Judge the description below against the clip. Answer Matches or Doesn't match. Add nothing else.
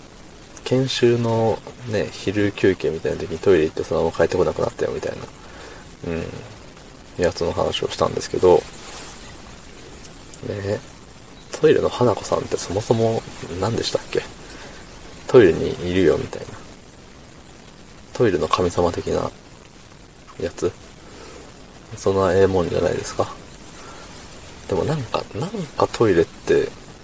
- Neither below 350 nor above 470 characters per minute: Doesn't match